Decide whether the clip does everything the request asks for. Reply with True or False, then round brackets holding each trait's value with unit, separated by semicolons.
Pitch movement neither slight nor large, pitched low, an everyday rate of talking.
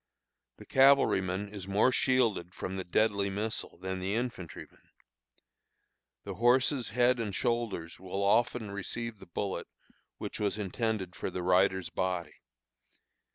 False (4.0 semitones; 100 Hz; 130 wpm)